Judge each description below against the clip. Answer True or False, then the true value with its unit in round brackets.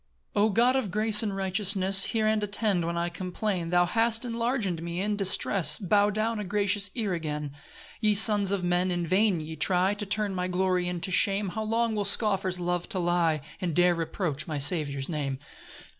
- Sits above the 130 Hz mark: True (190 Hz)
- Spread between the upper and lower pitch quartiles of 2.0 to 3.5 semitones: True (3.2 semitones)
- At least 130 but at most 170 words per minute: False (200 wpm)